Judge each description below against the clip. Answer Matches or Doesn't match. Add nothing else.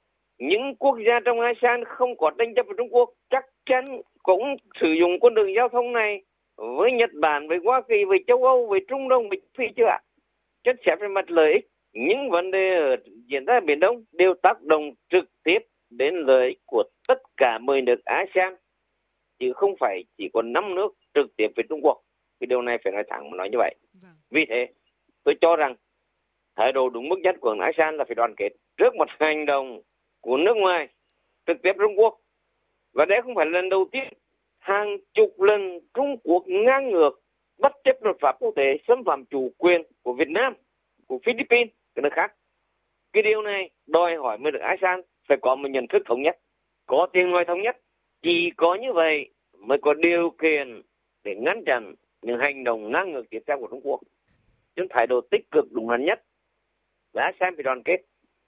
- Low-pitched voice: Doesn't match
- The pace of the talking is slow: Doesn't match